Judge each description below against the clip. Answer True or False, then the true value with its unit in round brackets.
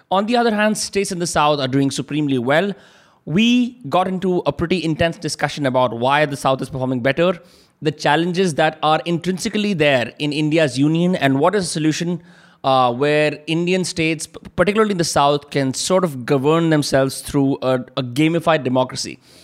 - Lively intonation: False (4.3 semitones)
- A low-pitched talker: False (155 Hz)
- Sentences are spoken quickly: False (180 wpm)